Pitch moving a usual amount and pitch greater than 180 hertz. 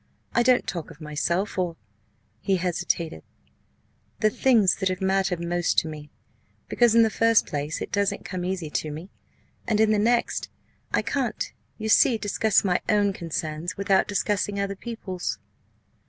Yes: average, 3.7 semitones; high, 190 Hz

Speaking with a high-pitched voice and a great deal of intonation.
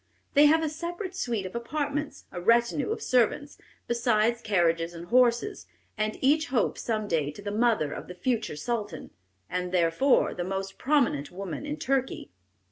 Yes: high, 235 Hz; wide, 7.5 semitones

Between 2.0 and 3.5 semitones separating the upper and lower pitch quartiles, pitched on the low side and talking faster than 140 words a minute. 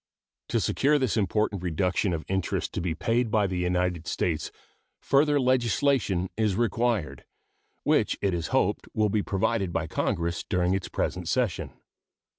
No: average, 4.7 semitones; very low, 95 Hz; average, 150 wpm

